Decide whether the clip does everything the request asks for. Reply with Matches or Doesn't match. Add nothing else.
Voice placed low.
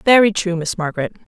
Doesn't match